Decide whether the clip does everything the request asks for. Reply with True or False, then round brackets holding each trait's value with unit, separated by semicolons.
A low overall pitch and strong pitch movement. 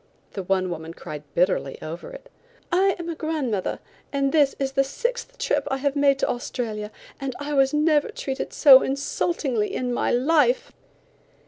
False (275 Hz; 5.7 semitones)